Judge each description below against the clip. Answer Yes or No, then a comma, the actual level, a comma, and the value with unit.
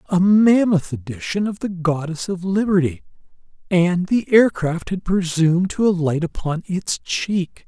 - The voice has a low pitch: No, medium, 180 Hz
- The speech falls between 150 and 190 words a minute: No, average, 140 wpm